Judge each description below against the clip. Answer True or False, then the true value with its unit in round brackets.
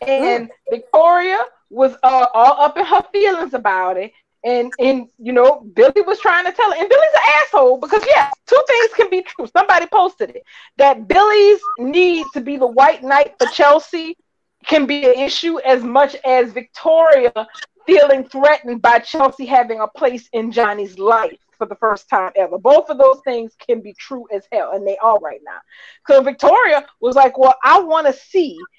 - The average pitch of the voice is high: True (275 Hz)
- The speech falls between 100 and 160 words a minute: False (190 wpm)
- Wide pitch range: True (6.2 semitones)